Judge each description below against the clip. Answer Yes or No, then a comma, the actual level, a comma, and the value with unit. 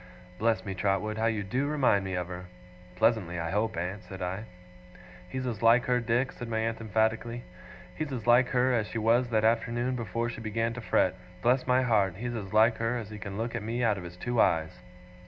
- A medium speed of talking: No, fast, 225 wpm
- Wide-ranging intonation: No, average, 3.0 semitones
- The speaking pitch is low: Yes, low, 115 Hz